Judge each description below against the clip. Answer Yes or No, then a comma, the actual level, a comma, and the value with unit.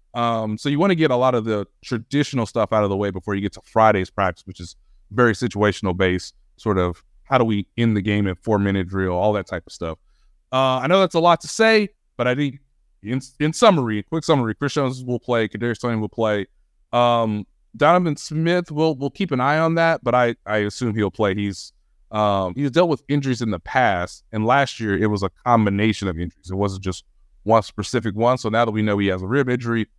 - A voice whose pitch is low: Yes, low, 110 Hz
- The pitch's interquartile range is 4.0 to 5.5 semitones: Yes, average, 4.7 semitones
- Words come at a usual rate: No, fast, 235 wpm